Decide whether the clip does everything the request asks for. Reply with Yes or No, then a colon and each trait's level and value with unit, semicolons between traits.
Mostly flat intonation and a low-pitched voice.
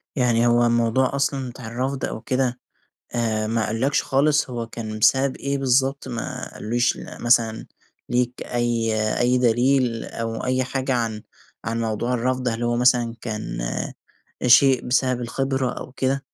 Yes: narrow, 2.2 semitones; low, 120 Hz